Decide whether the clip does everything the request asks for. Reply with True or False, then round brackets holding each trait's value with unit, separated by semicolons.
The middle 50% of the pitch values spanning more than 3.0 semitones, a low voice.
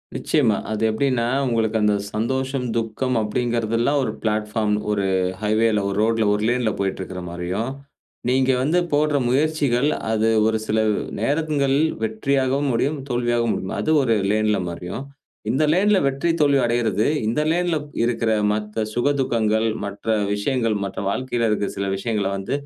True (3.9 semitones; 115 Hz)